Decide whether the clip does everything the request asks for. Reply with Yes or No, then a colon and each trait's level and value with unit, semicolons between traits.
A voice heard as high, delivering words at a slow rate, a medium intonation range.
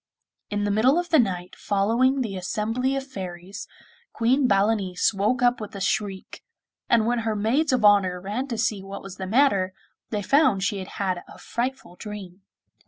No: high, 210 Hz; average, 180 wpm; average, 4.1 semitones